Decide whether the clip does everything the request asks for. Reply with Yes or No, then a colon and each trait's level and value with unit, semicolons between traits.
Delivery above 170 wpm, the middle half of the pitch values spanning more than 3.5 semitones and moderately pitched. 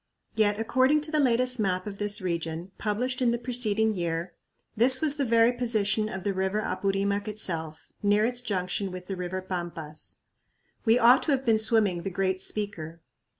No: average, 180 wpm; average, 4.2 semitones; high, 205 Hz